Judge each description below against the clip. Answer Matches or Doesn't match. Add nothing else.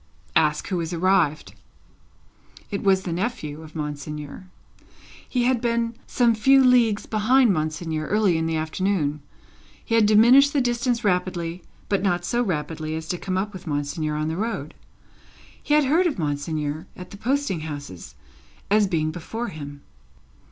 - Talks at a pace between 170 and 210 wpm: Doesn't match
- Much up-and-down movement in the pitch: Matches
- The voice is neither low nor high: Matches